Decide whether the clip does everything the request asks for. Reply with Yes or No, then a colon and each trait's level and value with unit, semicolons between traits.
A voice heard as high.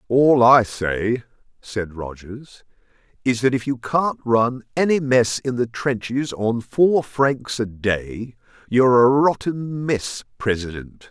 No: low, 120 Hz